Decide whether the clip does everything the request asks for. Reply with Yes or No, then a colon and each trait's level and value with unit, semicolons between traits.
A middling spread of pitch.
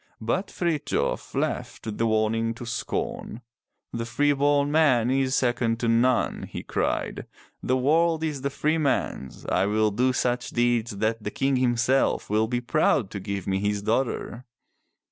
Yes: average, 3.7 semitones